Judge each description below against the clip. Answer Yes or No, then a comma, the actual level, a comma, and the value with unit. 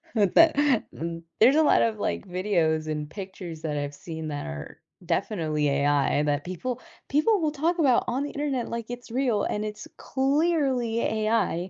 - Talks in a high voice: Yes, high, 215 Hz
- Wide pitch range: Yes, wide, 8.9 semitones